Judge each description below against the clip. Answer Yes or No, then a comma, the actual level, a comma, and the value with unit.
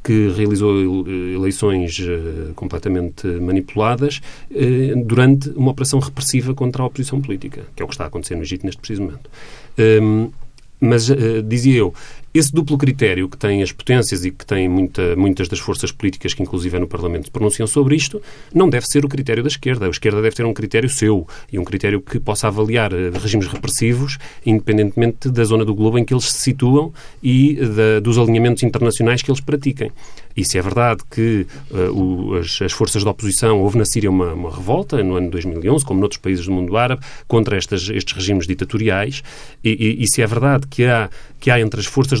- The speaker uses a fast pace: Yes, fast, 195 wpm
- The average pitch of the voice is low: Yes, low, 110 Hz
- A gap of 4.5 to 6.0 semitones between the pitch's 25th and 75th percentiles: Yes, average, 5.2 semitones